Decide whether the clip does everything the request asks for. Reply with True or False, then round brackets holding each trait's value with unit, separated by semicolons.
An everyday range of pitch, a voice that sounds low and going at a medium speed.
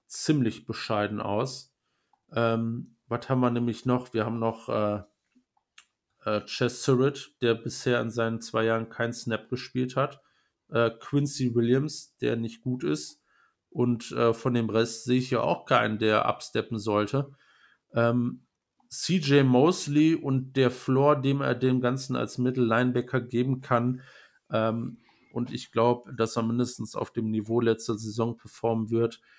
False (2.3 semitones; 120 Hz; 150 wpm)